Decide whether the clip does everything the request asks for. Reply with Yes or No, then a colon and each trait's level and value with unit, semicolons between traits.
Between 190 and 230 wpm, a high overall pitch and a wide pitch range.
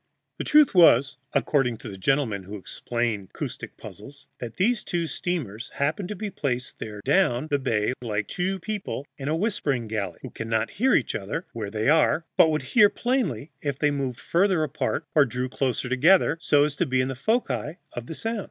No: average, 195 wpm; medium, 140 Hz; wide, 6.7 semitones